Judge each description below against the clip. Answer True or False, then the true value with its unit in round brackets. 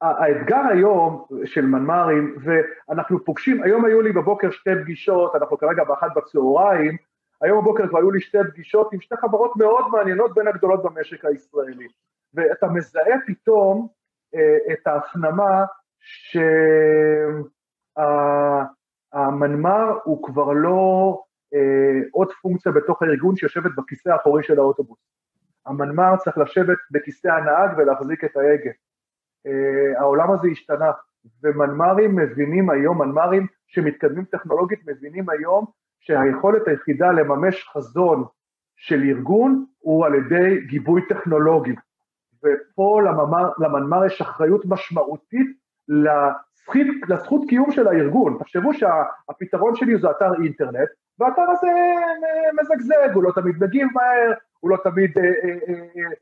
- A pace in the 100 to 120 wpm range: True (115 wpm)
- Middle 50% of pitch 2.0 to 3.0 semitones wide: False (5.6 semitones)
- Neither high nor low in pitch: True (180 Hz)